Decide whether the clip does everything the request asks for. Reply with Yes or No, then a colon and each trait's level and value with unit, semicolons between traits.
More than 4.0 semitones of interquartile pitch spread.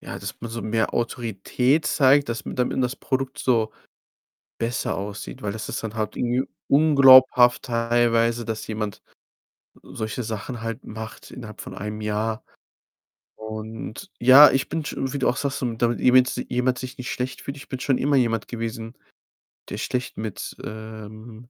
No: average, 2.8 semitones